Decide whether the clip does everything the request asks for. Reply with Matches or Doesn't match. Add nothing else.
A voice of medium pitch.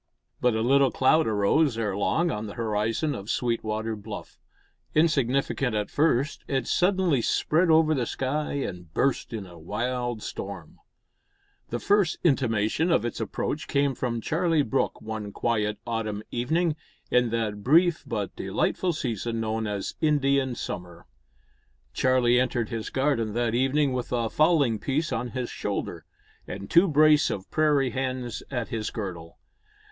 Doesn't match